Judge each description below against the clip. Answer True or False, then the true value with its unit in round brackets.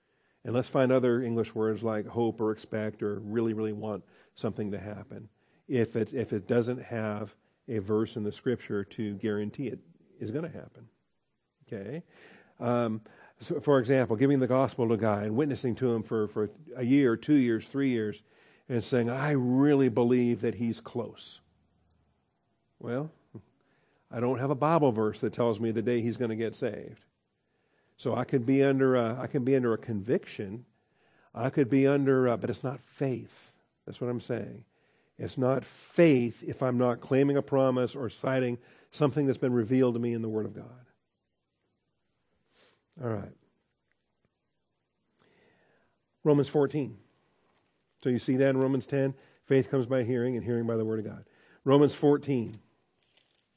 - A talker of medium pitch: False (120 Hz)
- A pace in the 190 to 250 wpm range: False (170 wpm)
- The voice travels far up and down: False (3.3 semitones)